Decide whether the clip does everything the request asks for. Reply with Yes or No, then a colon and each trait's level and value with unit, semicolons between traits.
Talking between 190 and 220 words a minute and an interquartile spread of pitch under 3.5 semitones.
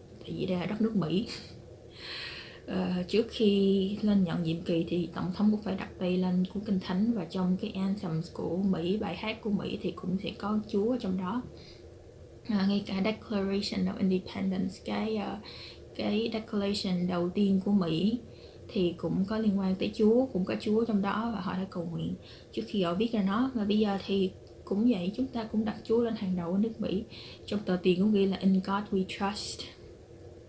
Yes: average, 205 wpm; average, 2.7 semitones